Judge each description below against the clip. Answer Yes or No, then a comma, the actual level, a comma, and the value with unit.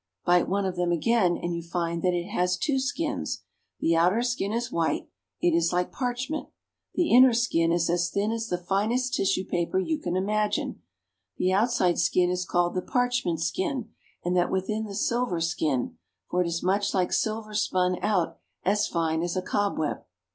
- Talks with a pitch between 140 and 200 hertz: Yes, medium, 185 Hz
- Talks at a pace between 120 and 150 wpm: No, average, 190 wpm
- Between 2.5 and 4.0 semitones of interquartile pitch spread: No, average, 4.5 semitones